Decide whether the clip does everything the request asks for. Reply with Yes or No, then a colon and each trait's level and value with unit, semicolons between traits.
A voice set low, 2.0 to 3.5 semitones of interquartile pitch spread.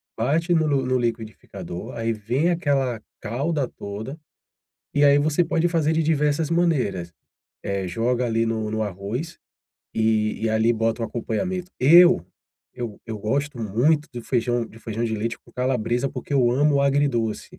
No: low, 125 Hz; average, 4.8 semitones